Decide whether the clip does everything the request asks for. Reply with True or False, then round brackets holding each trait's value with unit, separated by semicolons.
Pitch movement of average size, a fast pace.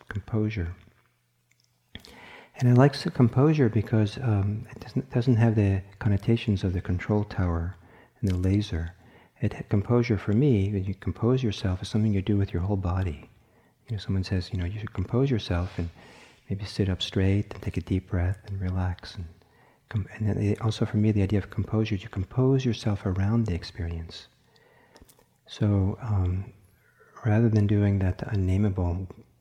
False (3.1 semitones; 170 wpm)